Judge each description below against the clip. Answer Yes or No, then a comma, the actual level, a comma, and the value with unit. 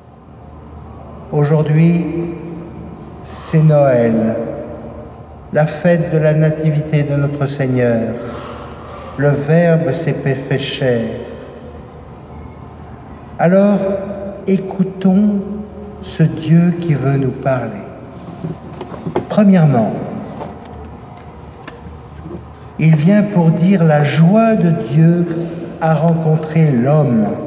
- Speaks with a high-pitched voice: No, medium, 155 Hz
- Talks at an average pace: No, slow, 80 wpm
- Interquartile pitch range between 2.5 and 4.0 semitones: Yes, average, 3.7 semitones